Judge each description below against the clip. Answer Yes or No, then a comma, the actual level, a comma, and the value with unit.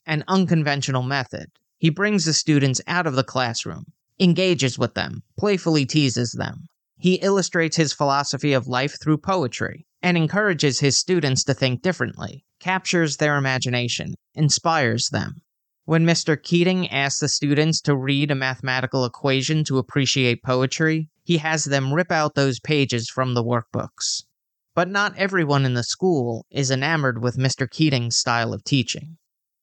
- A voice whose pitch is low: No, medium, 145 Hz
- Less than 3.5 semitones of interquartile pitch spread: No, average, 4.1 semitones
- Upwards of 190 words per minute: No, average, 150 wpm